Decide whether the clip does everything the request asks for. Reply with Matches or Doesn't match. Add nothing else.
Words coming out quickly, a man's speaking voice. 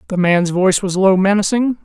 Doesn't match